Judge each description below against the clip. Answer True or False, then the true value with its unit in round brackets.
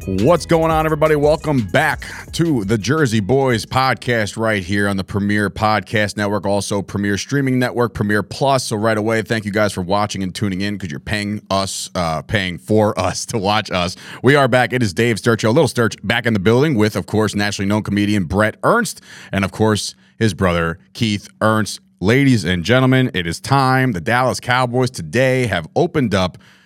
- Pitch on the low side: True (110 Hz)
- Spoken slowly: False (200 wpm)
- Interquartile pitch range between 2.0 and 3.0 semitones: False (3.8 semitones)